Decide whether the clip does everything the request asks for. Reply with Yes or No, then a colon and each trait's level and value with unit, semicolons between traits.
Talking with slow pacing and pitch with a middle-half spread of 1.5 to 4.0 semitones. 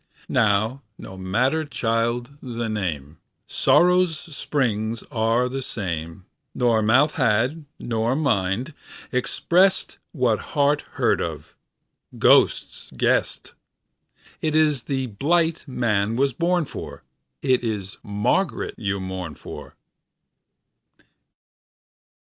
No: slow, 90 wpm; wide, 5.6 semitones